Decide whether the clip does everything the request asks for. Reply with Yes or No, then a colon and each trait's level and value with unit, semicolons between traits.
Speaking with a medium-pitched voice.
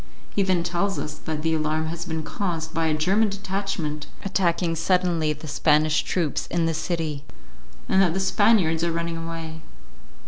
Yes: medium, 165 Hz